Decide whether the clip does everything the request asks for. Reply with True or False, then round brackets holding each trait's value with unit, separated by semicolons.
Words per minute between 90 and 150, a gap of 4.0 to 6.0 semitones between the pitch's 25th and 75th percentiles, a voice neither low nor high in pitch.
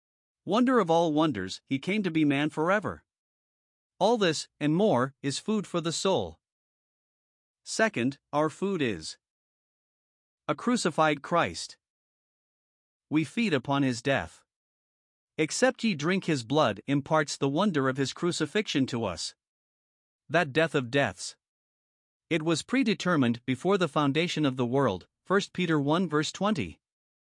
True (135 wpm; 4.8 semitones; 155 Hz)